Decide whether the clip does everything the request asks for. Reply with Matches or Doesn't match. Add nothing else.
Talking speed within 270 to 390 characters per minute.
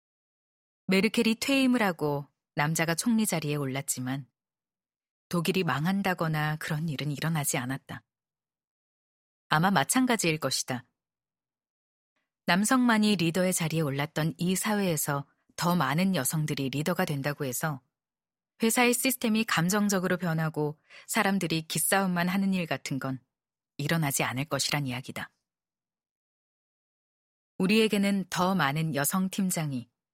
Matches